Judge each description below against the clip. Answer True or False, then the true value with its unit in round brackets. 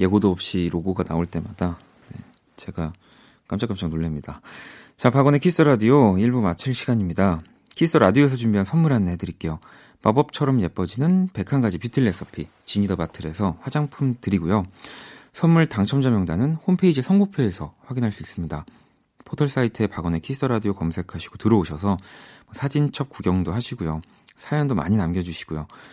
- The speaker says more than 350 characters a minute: True (370 characters per minute)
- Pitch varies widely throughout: True (7.5 semitones)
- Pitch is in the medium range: False (105 Hz)